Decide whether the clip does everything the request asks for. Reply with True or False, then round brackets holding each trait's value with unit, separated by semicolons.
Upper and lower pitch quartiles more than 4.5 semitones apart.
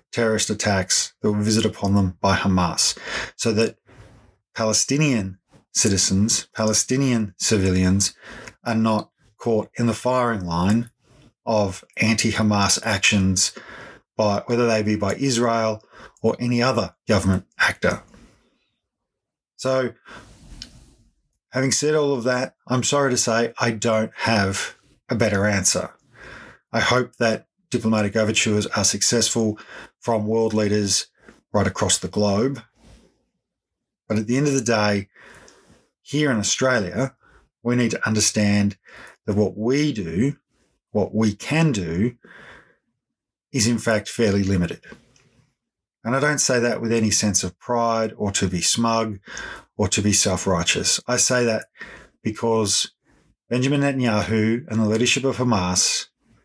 False (2.9 semitones)